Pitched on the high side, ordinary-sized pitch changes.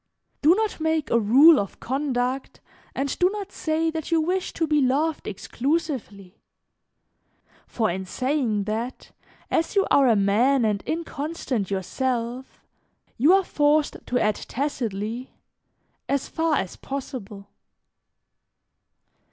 No: very high, 270 Hz; wide, 6.0 semitones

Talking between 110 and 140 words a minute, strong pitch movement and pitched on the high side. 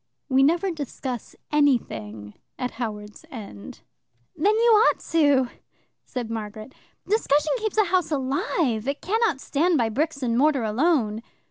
Yes: slow, 135 wpm; wide, 6.4 semitones; very high, 275 Hz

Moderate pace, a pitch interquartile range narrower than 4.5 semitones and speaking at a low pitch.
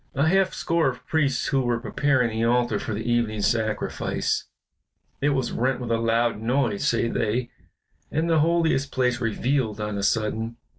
Yes: average, 170 wpm; average, 3.4 semitones; low, 120 Hz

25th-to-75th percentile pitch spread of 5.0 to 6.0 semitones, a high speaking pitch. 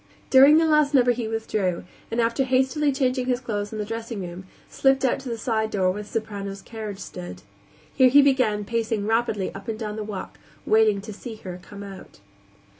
No: average, 3.8 semitones; high, 220 Hz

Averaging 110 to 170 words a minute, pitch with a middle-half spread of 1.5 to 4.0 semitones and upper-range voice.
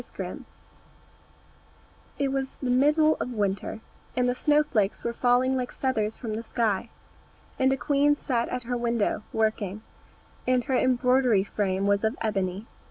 Yes: average, 165 wpm; average, 3.4 semitones; high, 245 Hz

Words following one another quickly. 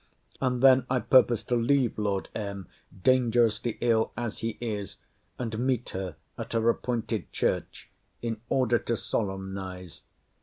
No: average, 140 wpm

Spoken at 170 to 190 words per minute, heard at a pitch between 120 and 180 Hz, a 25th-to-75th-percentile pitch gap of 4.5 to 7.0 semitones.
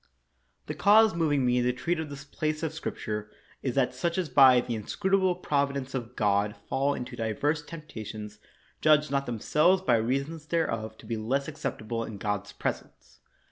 Yes: average, 175 wpm; low, 135 Hz; wide, 5.4 semitones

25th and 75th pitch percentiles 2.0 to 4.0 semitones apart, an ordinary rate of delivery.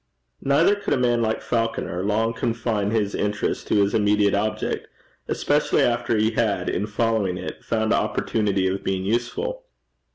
Yes: narrow, 2.4 semitones; average, 155 wpm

